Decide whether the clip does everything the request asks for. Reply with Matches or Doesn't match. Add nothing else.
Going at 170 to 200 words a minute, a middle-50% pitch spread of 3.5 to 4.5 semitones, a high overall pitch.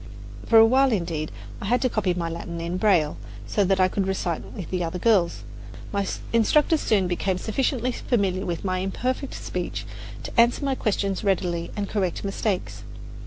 Matches